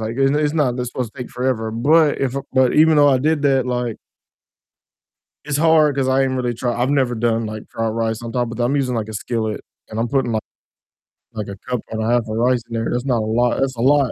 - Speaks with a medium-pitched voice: No, low, 125 Hz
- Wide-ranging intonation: No, average, 3.0 semitones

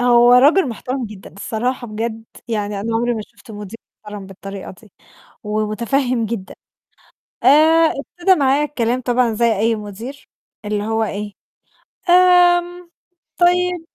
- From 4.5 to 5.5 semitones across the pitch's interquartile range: Yes, average, 5.0 semitones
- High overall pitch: Yes, high, 235 Hz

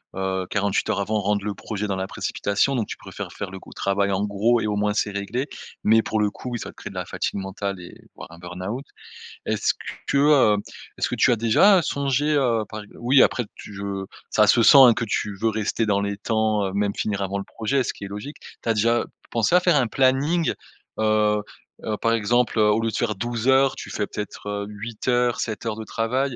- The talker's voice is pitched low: Yes, low, 110 Hz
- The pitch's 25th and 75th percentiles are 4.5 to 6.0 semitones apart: No, average, 3.0 semitones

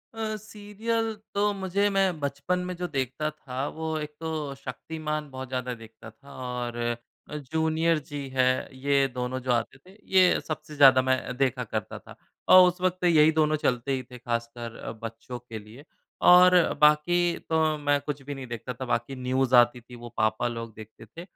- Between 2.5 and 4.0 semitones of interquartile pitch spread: No, average, 4.6 semitones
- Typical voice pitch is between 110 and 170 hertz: Yes, medium, 140 Hz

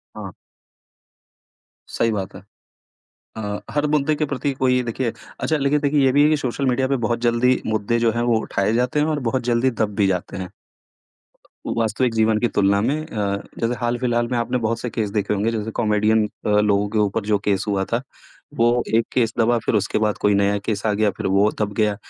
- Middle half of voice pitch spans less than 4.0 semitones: Yes, average, 3.1 semitones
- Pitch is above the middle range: No, low, 115 Hz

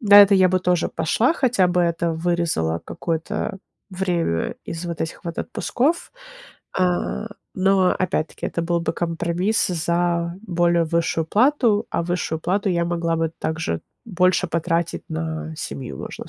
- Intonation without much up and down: Yes, narrow, 2.0 semitones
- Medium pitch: Yes, medium, 170 Hz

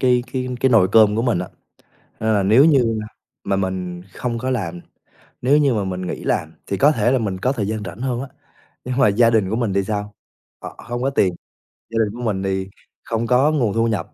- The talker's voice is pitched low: Yes, low, 110 Hz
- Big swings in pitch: No, average, 4.3 semitones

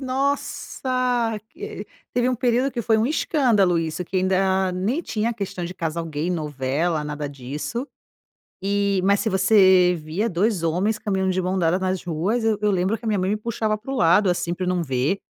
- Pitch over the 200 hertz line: No, high, 190 Hz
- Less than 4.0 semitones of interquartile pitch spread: No, average, 4.4 semitones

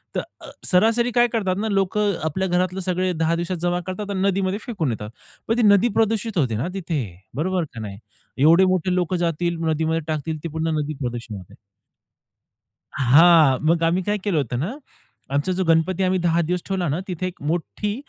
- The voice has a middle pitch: Yes, medium, 175 Hz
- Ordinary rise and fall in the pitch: Yes, average, 3.2 semitones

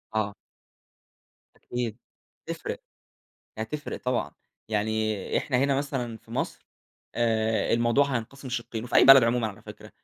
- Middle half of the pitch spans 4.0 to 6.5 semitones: No, average, 2.9 semitones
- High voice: No, low, 120 Hz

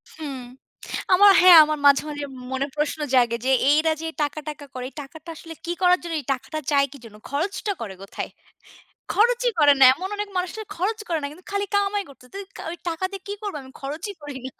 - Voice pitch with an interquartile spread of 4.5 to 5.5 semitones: Yes, average, 5.2 semitones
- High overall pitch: Yes, very high, 315 Hz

